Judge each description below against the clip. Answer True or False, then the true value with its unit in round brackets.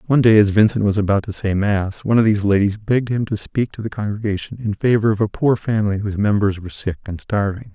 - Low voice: True (105 Hz)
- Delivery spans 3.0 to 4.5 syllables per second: False (6.6 syllables/s)